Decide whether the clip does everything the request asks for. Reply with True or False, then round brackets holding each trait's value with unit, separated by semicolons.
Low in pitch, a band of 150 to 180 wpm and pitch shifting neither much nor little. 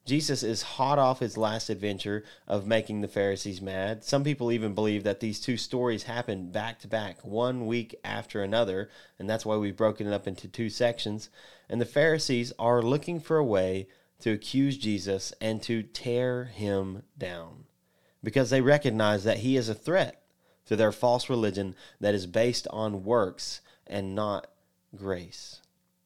True (110 Hz; 170 wpm; 3.0 semitones)